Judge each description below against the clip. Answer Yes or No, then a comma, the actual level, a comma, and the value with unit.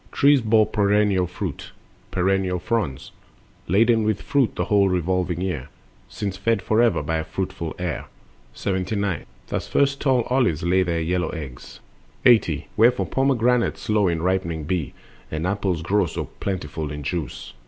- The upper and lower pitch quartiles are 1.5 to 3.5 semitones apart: No, average, 4.4 semitones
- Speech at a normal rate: Yes, average, 145 wpm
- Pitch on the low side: Yes, very low, 95 Hz